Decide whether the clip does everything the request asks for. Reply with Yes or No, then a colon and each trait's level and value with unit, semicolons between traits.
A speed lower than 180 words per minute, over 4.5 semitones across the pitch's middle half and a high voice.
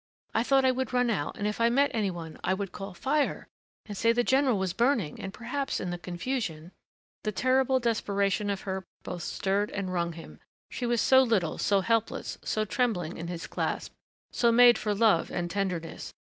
No: fast, 205 wpm; average, 4.9 semitones; high, 210 Hz